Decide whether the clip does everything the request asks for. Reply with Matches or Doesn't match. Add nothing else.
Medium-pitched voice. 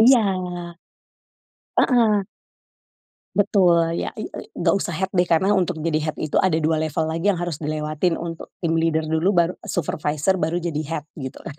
Matches